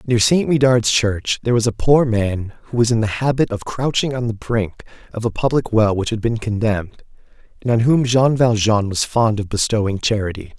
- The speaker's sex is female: No, male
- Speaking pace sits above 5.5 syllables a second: No, 5.2 syllables/s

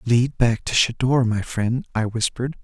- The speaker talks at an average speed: Yes, average, 180 wpm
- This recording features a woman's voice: No, male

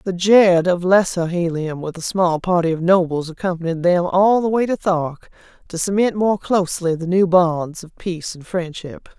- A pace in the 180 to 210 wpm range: Yes, average, 190 wpm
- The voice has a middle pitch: Yes, medium, 175 Hz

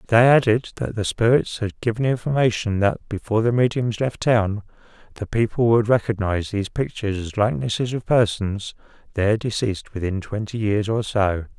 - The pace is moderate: Yes, average, 160 wpm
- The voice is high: No, low, 110 Hz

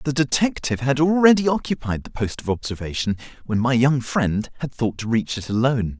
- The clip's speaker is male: Yes, male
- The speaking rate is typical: Yes, average, 190 wpm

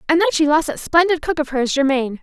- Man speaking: No, female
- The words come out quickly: Yes, fast, 270 wpm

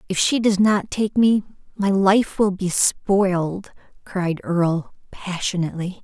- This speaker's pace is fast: No, average, 140 wpm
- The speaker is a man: No, female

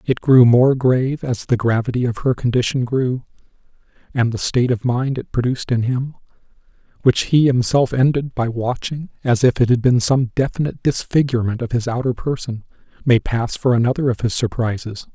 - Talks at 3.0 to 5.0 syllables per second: No, 5.4 syllables/s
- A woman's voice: No, male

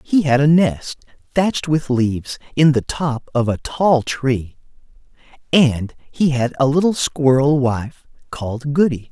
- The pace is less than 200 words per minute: Yes, average, 150 wpm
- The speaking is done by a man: Yes, male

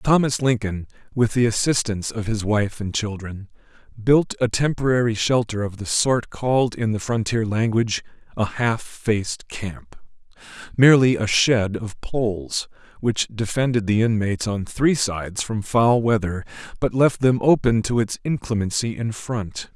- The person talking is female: No, male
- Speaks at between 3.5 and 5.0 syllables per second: Yes, 4.6 syllables/s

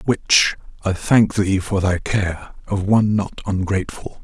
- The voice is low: Yes, low, 100 Hz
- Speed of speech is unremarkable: Yes, average, 155 wpm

